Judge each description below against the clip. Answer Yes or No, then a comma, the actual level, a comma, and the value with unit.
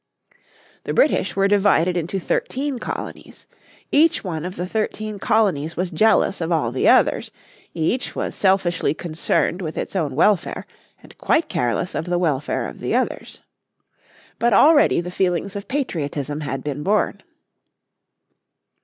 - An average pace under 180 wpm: Yes, average, 145 wpm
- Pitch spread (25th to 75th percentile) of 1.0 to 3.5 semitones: No, average, 4.7 semitones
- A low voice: No, medium, 180 Hz